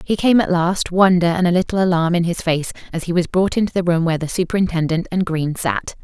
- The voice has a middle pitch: Yes, medium, 175 Hz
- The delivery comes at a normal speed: No, fast, 250 wpm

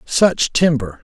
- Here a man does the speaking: Yes, male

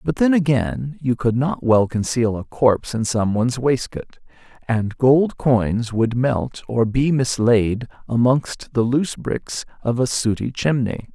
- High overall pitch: No, low, 120 Hz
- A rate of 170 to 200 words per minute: No, average, 155 wpm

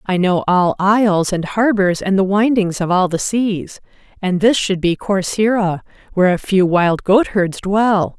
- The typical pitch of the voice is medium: No, high, 195 Hz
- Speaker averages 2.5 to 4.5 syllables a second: Yes, 4.2 syllables/s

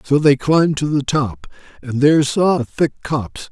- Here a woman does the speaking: No, male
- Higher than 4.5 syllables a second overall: Yes, 4.9 syllables/s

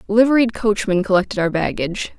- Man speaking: No, female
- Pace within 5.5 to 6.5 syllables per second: Yes, 6.0 syllables/s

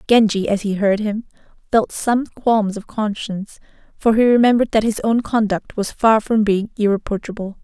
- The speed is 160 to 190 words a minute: Yes, average, 175 wpm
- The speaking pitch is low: No, high, 215 Hz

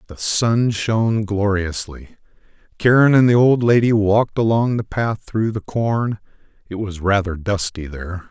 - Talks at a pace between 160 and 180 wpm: No, average, 150 wpm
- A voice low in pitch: Yes, low, 105 Hz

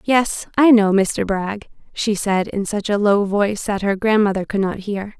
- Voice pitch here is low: No, high, 205 Hz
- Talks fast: Yes, fast, 210 wpm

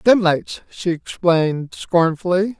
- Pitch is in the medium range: Yes, medium, 175 Hz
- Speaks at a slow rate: Yes, slow, 90 wpm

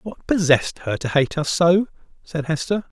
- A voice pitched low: No, medium, 165 Hz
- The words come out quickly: No, average, 180 wpm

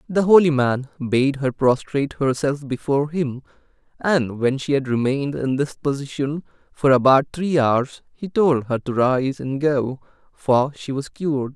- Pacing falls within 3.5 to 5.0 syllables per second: Yes, 4.5 syllables/s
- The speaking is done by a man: Yes, male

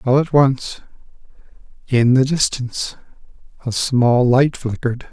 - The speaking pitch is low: Yes, low, 130 Hz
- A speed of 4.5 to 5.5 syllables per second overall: No, 4.3 syllables/s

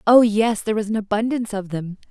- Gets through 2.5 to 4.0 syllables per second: No, 6.5 syllables/s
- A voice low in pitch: No, high, 215 Hz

